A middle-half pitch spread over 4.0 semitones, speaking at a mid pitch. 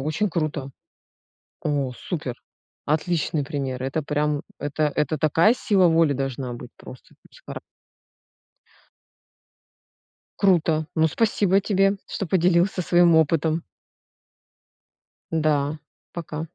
No: average, 3.3 semitones; medium, 155 Hz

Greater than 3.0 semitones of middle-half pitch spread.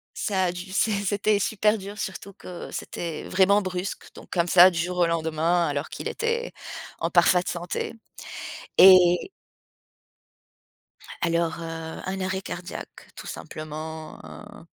No: average, 2.7 semitones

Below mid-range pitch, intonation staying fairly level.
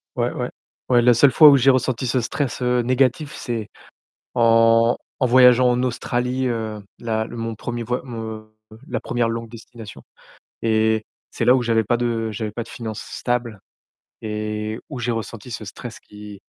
Yes: low, 115 Hz; narrow, 2.0 semitones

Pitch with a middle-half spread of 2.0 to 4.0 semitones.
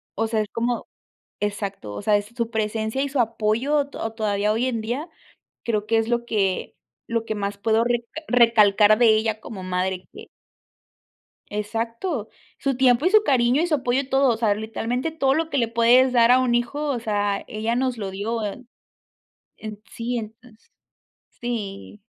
Yes: average, 2.7 semitones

